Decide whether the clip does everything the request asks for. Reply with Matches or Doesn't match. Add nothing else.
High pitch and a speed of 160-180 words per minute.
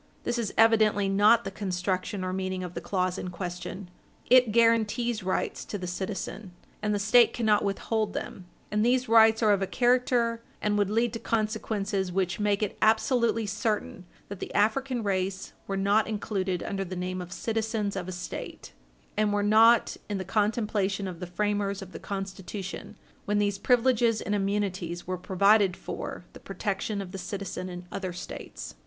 Matches